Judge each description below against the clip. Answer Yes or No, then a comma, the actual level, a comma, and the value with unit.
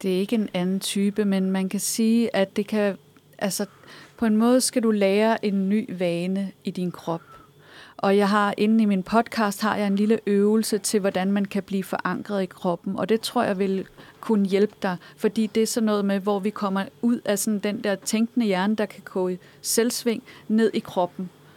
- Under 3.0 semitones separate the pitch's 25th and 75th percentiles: Yes, narrow, 2.4 semitones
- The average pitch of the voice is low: No, high, 205 Hz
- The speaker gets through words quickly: No, average, 215 wpm